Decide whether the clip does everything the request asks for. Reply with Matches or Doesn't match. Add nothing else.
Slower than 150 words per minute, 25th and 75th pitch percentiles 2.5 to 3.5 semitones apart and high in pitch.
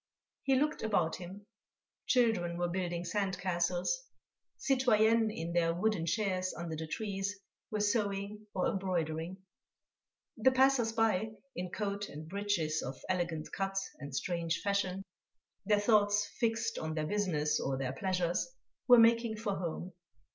Doesn't match